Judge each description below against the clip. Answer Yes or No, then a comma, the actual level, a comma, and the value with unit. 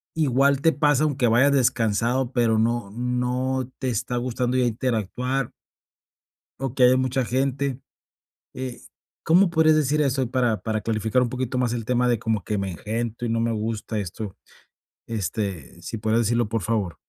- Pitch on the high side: No, low, 120 Hz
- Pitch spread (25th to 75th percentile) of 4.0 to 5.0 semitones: No, average, 2.7 semitones